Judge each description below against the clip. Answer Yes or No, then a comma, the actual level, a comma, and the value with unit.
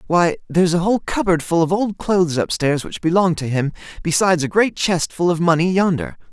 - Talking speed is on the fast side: Yes, fast, 220 wpm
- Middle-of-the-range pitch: Yes, medium, 170 Hz